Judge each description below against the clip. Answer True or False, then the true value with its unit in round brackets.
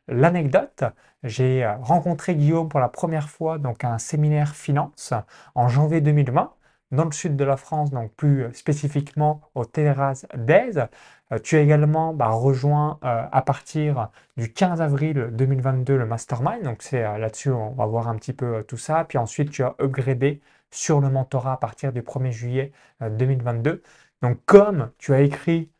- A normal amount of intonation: True (3.3 semitones)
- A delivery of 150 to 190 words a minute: True (175 wpm)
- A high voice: False (140 Hz)